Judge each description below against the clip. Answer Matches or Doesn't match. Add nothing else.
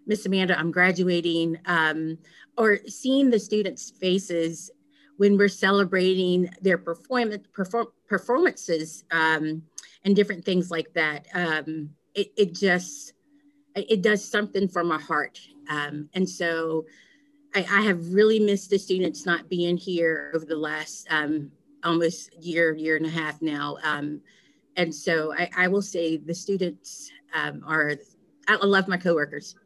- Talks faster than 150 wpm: Doesn't match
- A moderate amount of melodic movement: Matches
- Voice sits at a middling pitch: Matches